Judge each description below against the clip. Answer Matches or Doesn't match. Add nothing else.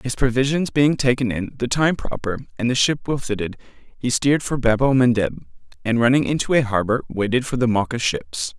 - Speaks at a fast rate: Doesn't match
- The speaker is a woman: Doesn't match